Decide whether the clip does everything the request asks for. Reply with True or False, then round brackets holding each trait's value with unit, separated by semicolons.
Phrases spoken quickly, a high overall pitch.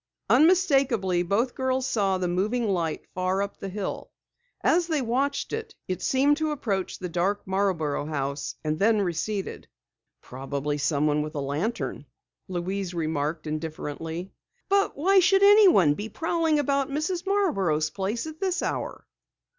False (140 wpm; 200 Hz)